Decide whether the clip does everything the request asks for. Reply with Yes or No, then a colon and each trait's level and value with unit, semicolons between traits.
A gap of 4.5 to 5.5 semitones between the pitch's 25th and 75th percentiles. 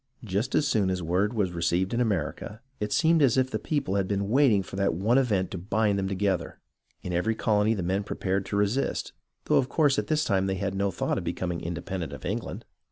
No: average, 3.4 semitones